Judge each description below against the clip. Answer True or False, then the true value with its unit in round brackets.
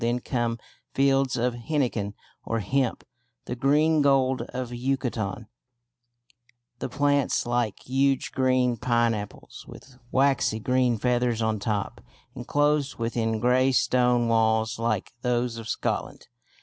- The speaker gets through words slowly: True (120 wpm)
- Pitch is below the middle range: True (125 Hz)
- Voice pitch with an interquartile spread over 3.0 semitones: False (2.5 semitones)